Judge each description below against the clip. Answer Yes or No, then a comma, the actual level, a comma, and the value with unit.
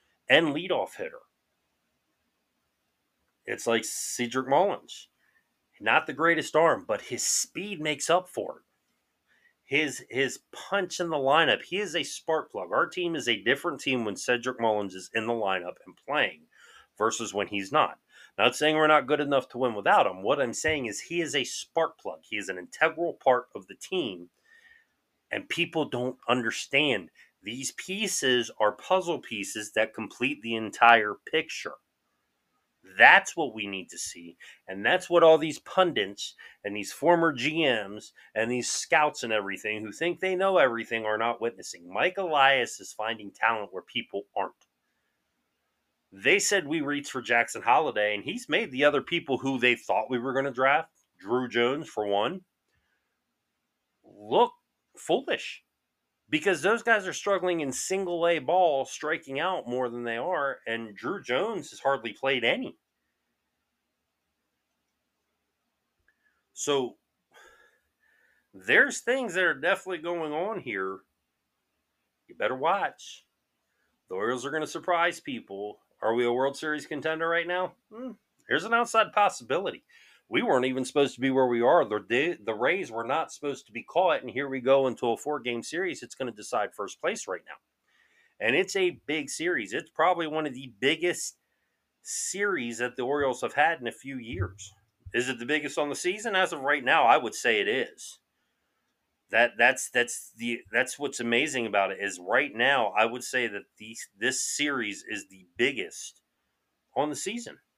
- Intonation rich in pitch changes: Yes, wide, 7.0 semitones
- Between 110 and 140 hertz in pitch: Yes, low, 135 Hz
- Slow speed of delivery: No, average, 170 wpm